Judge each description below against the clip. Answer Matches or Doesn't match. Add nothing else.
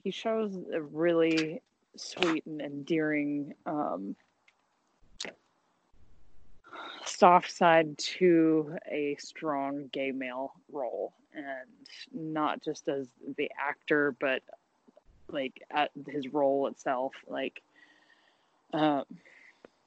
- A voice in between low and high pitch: Matches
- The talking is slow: Matches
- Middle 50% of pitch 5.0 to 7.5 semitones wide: Doesn't match